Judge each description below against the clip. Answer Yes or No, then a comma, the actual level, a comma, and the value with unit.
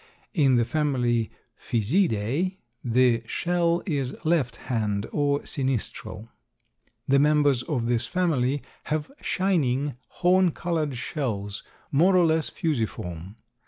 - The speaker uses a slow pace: Yes, slow, 110 wpm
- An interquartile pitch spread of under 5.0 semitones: No, wide, 5.5 semitones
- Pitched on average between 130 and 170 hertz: Yes, medium, 140 Hz